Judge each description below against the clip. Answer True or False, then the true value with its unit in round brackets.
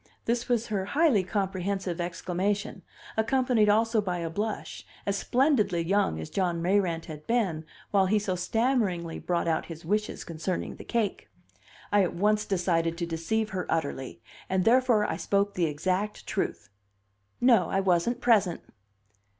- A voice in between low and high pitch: False (195 Hz)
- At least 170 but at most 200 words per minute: False (150 wpm)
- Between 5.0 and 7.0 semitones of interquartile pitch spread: False (4.1 semitones)